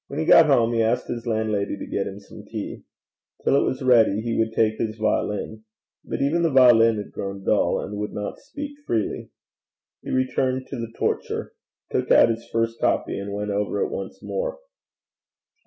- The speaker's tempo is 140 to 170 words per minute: No, average, 190 wpm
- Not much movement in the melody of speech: No, average, 3.6 semitones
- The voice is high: No, low, 115 Hz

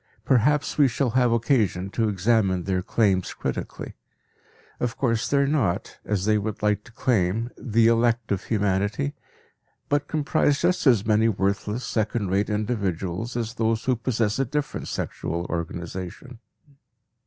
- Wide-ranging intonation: No, average, 3.7 semitones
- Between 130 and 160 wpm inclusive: Yes, average, 145 wpm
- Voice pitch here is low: Yes, low, 110 Hz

